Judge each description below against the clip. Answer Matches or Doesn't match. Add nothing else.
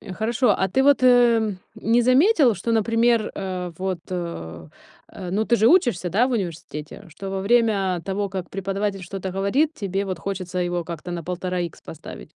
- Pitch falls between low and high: Doesn't match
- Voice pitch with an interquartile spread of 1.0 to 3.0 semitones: Doesn't match